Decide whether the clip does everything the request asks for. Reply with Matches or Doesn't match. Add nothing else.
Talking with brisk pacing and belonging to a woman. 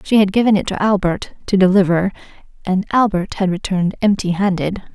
Doesn't match